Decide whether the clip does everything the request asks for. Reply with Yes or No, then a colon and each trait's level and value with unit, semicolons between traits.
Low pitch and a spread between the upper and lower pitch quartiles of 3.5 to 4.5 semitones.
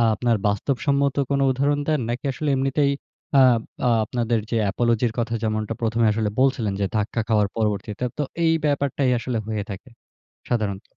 Yes: low, 120 Hz; average, 3.9 semitones